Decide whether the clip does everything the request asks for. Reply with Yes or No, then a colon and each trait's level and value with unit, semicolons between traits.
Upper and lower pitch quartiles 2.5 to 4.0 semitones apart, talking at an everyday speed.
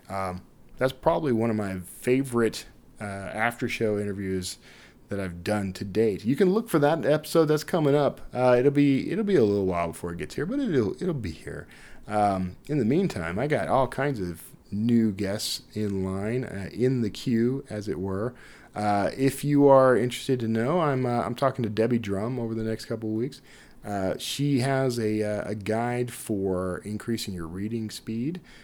No: average, 4.6 semitones; average, 195 wpm